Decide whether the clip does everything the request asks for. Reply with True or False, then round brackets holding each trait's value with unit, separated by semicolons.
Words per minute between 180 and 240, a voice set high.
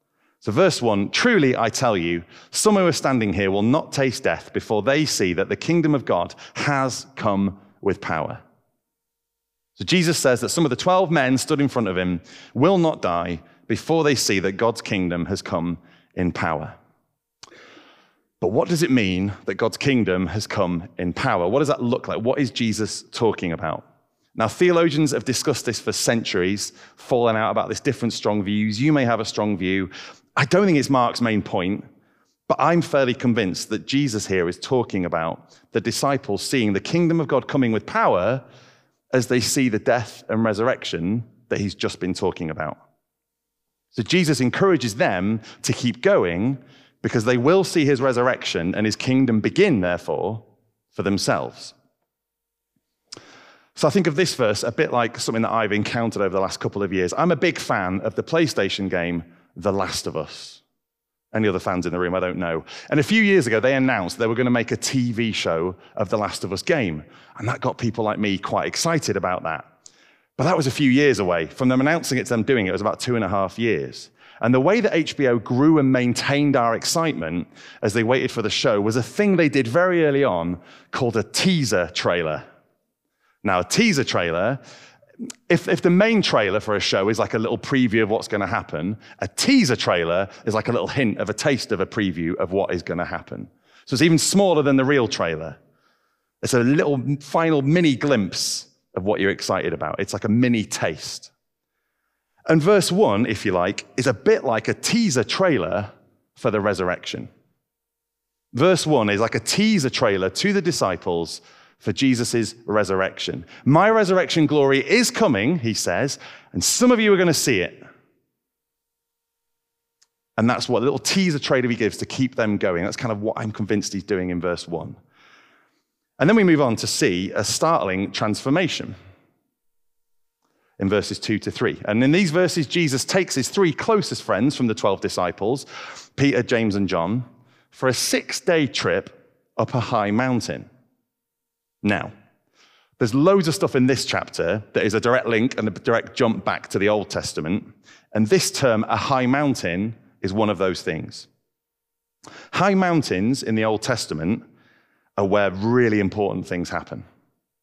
False (190 wpm; 120 Hz)